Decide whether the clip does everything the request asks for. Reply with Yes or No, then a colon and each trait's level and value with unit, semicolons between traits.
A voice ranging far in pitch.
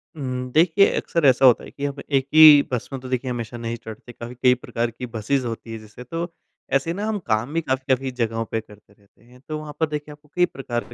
No: average, 4.0 semitones